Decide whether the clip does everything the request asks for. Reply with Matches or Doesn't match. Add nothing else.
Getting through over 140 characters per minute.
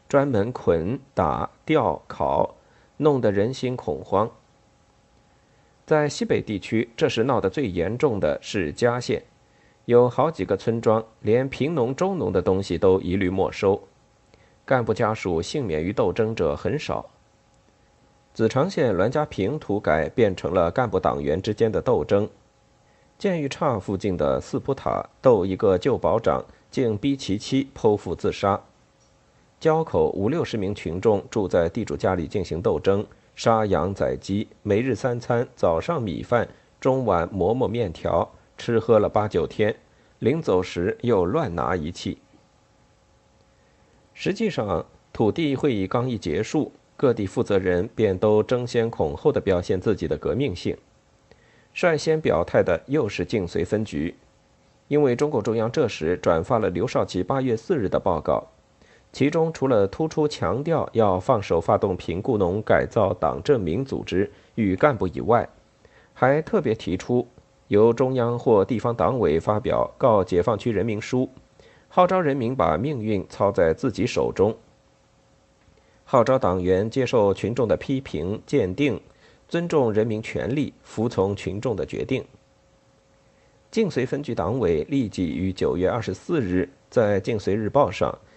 Matches